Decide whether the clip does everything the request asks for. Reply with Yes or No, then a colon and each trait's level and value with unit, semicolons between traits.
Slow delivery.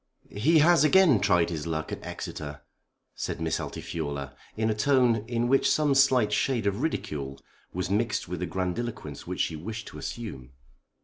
No: average, 170 wpm